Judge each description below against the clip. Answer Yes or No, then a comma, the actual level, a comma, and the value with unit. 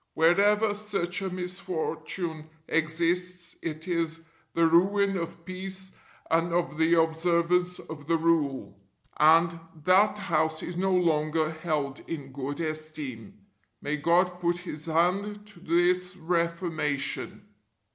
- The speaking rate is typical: No, slow, 120 wpm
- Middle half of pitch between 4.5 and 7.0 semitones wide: No, narrow, 2.4 semitones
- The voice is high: No, medium, 170 Hz